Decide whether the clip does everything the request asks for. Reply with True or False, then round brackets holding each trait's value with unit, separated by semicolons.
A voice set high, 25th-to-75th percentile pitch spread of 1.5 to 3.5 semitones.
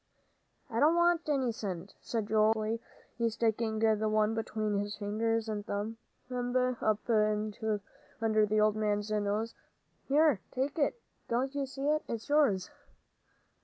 True (220 Hz; 3.0 semitones)